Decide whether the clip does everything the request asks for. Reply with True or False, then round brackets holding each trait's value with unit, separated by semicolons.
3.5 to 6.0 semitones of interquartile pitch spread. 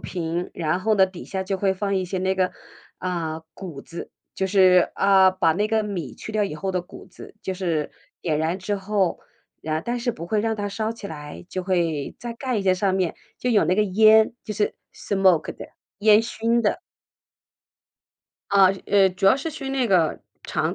False (2.9 semitones)